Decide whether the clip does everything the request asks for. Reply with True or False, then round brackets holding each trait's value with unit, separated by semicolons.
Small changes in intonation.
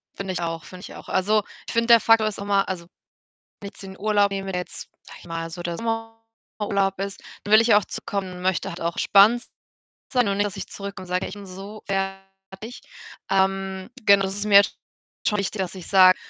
True (1.7 semitones)